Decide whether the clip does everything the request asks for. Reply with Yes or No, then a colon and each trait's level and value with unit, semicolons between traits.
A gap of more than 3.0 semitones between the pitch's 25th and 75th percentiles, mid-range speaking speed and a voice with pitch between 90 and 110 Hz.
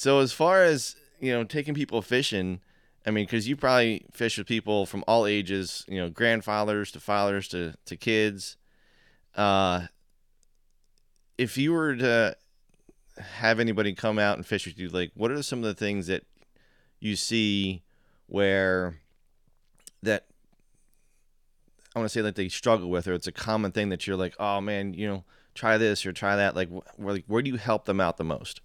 Yes: average, 3.6 semitones; average, 185 wpm; low, 105 Hz